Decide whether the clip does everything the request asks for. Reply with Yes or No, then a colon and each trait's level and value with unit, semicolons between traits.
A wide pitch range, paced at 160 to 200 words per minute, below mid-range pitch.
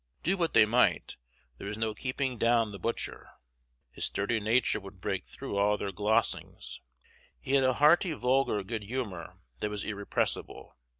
No: average, 4.1 semitones; average, 165 wpm; low, 110 Hz